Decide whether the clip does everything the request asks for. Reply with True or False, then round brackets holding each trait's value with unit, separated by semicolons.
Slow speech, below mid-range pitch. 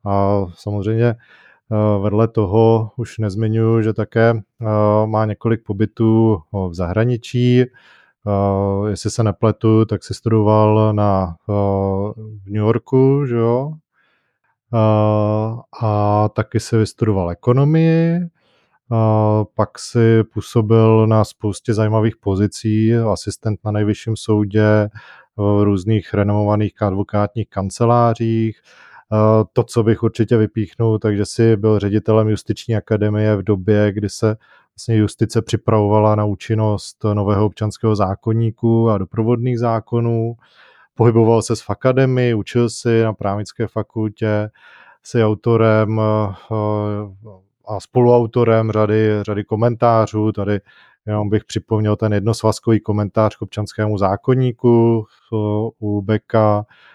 True (105 wpm; 110 Hz)